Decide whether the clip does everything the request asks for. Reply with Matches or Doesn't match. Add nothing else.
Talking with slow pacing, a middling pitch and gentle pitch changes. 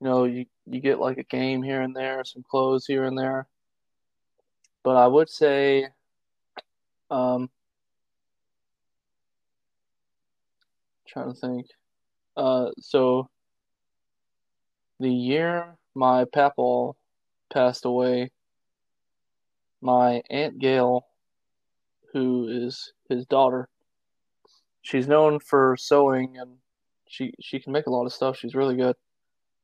Doesn't match